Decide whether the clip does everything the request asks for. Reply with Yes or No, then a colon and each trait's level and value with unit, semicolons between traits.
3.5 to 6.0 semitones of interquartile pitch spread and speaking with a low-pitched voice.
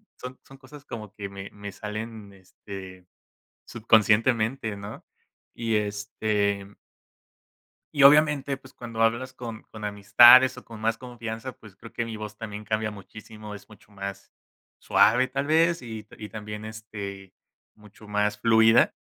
No: narrow, 2.4 semitones; low, 110 Hz